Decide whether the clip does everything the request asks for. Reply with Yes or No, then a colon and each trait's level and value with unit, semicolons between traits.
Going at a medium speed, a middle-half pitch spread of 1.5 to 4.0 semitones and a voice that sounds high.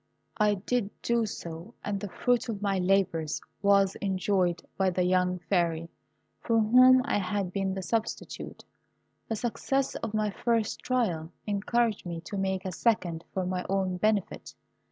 Yes: average, 155 wpm; average, 3.3 semitones; high, 195 Hz